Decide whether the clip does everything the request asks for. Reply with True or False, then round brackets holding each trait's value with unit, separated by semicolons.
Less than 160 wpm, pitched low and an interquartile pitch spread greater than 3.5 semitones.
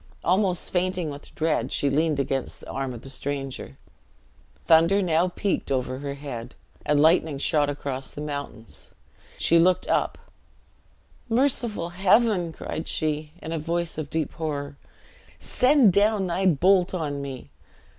False (145 wpm; 160 Hz; 4.3 semitones)